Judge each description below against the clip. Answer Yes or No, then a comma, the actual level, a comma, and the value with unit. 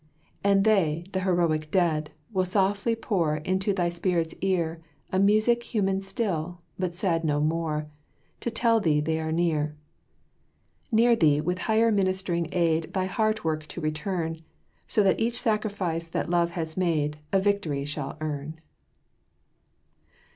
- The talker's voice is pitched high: No, medium, 175 Hz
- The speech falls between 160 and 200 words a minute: No, average, 145 wpm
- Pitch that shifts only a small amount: No, average, 3.9 semitones